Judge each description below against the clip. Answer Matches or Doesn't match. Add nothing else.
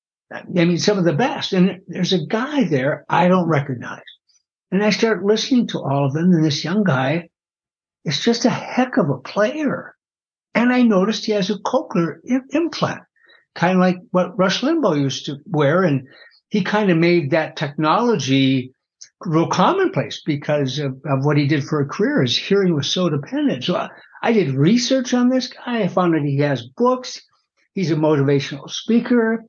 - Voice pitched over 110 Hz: Matches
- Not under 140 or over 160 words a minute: Doesn't match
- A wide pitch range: Matches